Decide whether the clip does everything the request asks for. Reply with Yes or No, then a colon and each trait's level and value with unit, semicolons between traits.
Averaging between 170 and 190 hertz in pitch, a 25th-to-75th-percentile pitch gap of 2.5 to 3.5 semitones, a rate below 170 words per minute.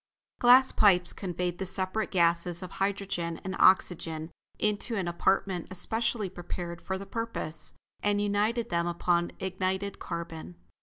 Yes: medium, 185 Hz; average, 2.9 semitones; slow, 135 wpm